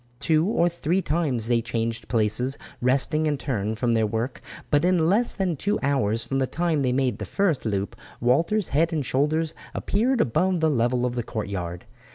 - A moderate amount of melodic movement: No, wide, 6.1 semitones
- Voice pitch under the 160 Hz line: Yes, low, 135 Hz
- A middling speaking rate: Yes, average, 190 wpm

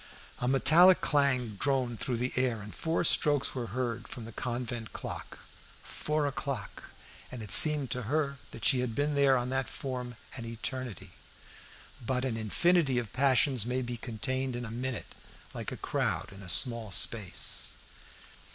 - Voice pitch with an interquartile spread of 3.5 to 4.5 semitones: No, average, 2.9 semitones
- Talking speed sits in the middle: Yes, average, 165 wpm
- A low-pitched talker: Yes, low, 125 Hz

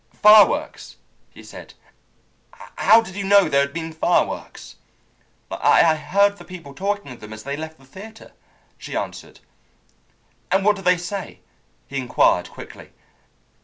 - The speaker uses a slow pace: No, average, 145 wpm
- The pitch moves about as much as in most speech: No, wide, 6.1 semitones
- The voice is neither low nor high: Yes, medium, 180 Hz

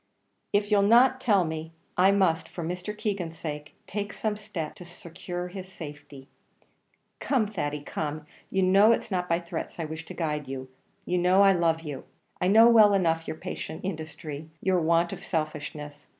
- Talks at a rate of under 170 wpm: No, average, 180 wpm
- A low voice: No, medium, 175 Hz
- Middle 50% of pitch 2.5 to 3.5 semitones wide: No, average, 4.0 semitones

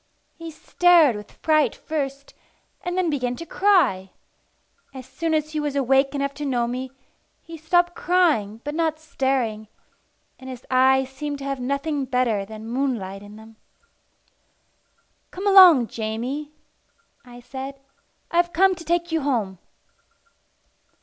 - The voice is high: Yes, very high, 275 Hz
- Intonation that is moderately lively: Yes, average, 4.7 semitones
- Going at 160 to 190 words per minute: No, average, 140 wpm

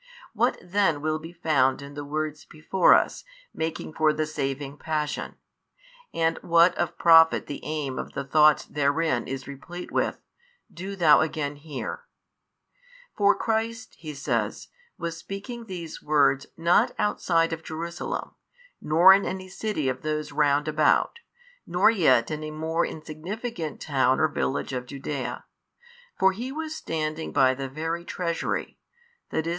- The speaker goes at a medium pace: Yes, average, 150 wpm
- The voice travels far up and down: No, average, 3.1 semitones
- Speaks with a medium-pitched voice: Yes, medium, 155 Hz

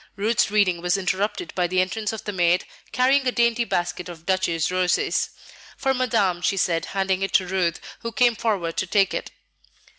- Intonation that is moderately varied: Yes, average, 4.0 semitones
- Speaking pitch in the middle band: No, high, 195 Hz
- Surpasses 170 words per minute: Yes, average, 185 wpm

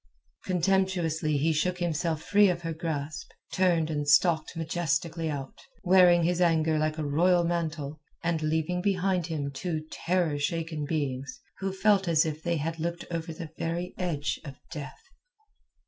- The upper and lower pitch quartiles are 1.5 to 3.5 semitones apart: Yes, narrow, 2.4 semitones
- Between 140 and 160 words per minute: Yes, average, 155 wpm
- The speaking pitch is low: No, medium, 165 Hz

